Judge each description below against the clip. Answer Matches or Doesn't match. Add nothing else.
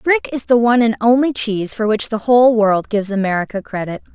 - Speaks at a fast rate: Matches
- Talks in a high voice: Matches